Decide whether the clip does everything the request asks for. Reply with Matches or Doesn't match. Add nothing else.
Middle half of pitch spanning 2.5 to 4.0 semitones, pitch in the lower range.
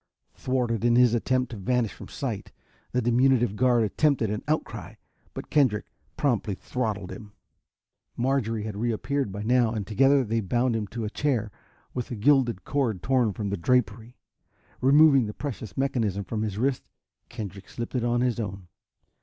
Matches